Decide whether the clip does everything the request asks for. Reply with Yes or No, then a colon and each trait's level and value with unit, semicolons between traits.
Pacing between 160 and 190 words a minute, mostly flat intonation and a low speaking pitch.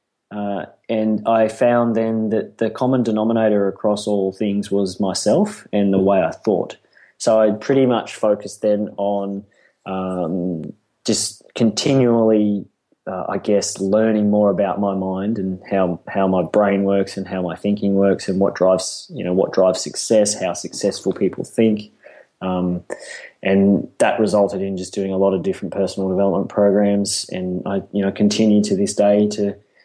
Yes: average, 165 wpm; narrow, 1.8 semitones; low, 100 Hz